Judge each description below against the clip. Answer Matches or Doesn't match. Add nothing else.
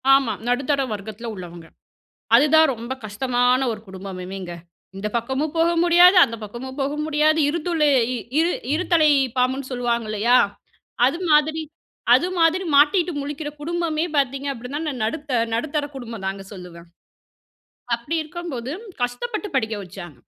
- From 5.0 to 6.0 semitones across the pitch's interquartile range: Matches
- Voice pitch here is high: Matches